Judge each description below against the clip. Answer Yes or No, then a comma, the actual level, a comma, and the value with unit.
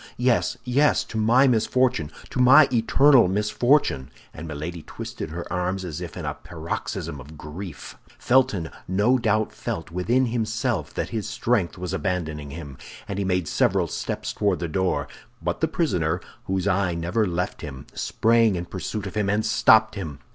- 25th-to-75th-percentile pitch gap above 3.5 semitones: Yes, average, 5.0 semitones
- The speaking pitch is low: Yes, low, 100 Hz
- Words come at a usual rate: Yes, average, 170 wpm